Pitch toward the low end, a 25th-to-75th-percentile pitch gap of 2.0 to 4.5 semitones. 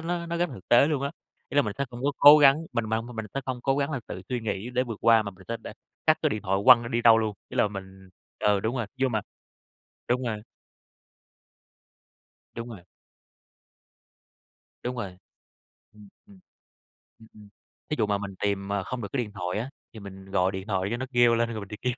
Yes: low, 115 Hz; average, 3.9 semitones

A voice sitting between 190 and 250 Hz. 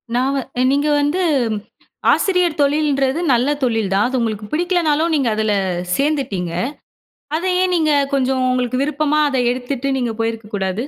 No: very high, 270 Hz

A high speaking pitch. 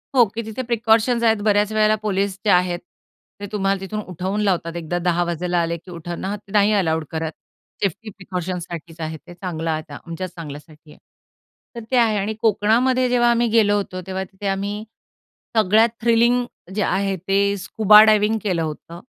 Yes: high, 195 Hz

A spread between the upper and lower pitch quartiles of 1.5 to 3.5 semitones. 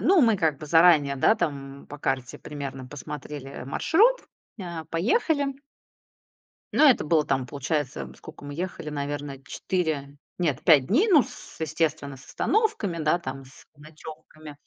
No: average, 4.1 semitones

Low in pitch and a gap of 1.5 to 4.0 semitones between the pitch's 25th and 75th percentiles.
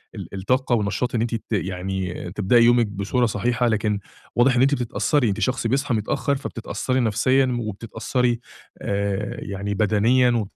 Yes: low, 115 Hz; average, 3.5 semitones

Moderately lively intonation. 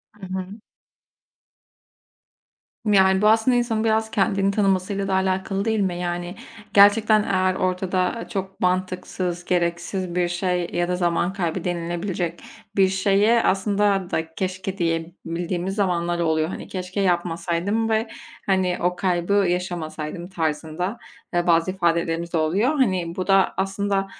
No: narrow, 2.2 semitones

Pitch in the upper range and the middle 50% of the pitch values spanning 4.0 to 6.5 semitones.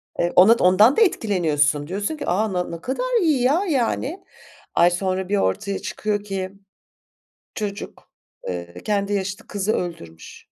Yes: high, 200 Hz; average, 4.6 semitones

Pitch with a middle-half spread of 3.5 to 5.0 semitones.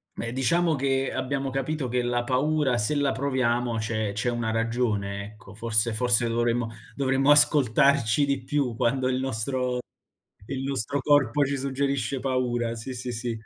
No: average, 2.8 semitones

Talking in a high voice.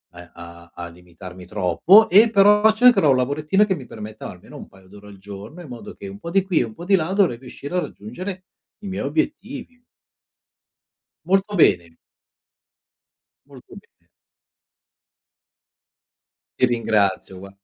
No: low, 130 Hz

